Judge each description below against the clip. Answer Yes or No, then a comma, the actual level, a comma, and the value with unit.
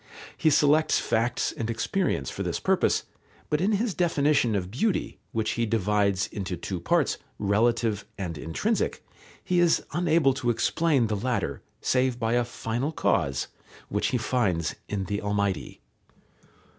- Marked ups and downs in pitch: Yes, wide, 6.5 semitones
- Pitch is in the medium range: No, low, 115 Hz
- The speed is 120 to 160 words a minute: Yes, average, 145 wpm